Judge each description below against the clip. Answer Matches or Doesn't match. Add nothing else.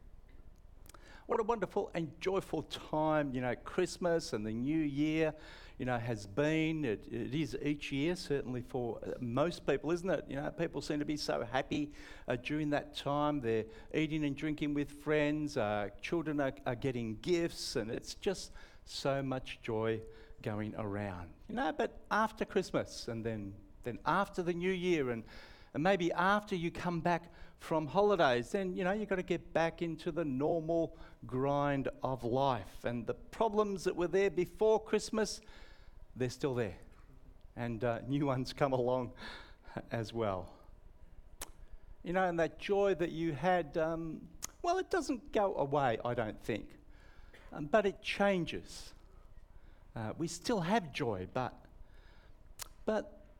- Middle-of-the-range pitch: Matches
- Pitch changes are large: Matches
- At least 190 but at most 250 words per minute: Doesn't match